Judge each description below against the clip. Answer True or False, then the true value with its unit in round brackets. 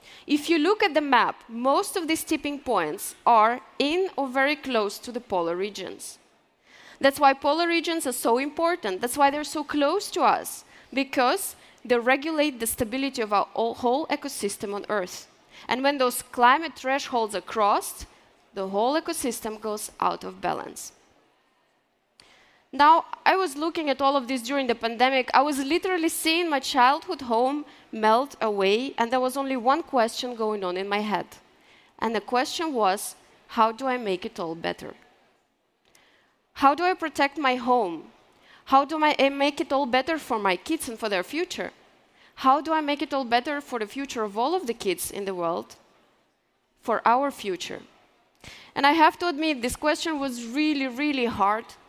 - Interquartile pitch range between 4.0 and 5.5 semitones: True (4.7 semitones)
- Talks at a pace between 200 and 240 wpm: False (175 wpm)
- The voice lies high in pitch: True (265 Hz)